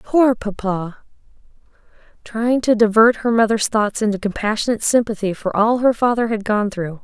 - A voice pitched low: No, high, 220 Hz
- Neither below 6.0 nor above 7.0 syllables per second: No, 5.1 syllables/s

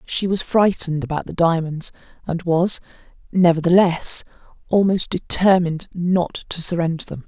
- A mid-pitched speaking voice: Yes, medium, 170 Hz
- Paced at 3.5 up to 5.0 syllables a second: Yes, 4.8 syllables/s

